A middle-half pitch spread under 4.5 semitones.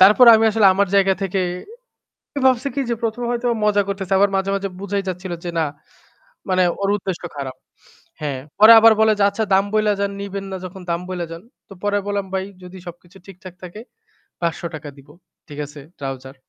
Yes: average, 2.9 semitones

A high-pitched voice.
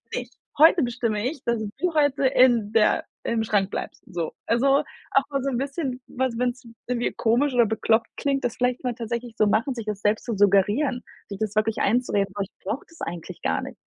Yes: high, 240 Hz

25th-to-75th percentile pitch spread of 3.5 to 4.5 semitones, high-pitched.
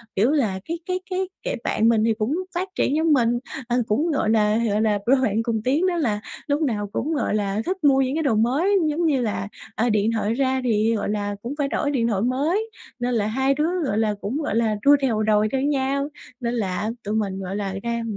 No: average, 5.1 semitones; high, 235 Hz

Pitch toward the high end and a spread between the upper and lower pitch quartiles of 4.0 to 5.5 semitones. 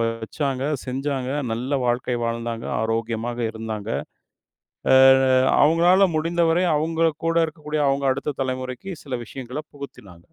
No: low, 130 Hz; average, 4.8 semitones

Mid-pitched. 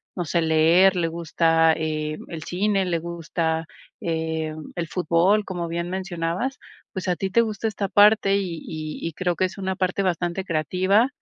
Yes: medium, 175 Hz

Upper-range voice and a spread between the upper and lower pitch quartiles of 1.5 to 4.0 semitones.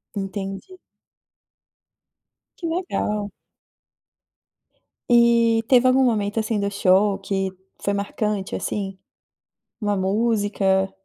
Yes: high, 205 Hz; average, 3.0 semitones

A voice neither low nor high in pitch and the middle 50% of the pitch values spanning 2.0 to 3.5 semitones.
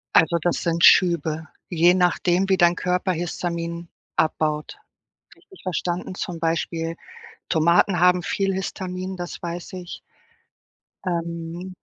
No: medium, 175 Hz; narrow, 1.5 semitones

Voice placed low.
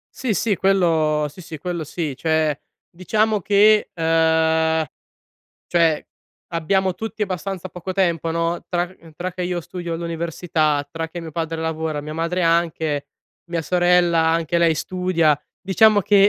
No: medium, 170 Hz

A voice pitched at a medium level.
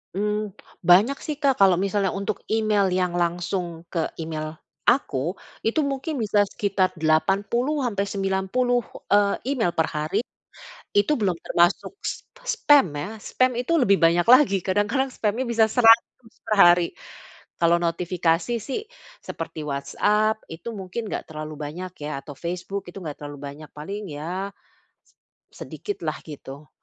No: high, 195 Hz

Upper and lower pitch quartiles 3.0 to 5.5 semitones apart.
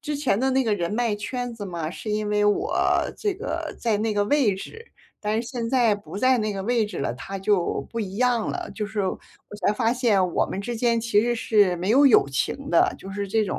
Yes: average, 3.3 semitones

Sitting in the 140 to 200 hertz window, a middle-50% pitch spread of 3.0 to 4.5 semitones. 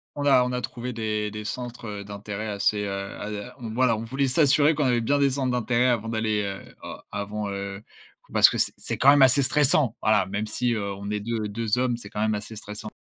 No: low, 110 Hz; average, 3.4 semitones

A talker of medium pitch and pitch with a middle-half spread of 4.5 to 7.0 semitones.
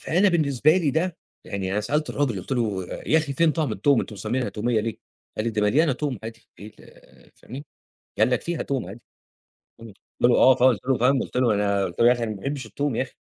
No: low, 125 Hz; average, 4.9 semitones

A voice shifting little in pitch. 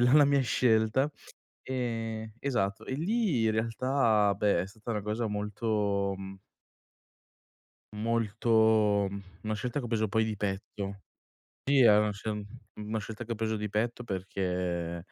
Yes: narrow, 2.3 semitones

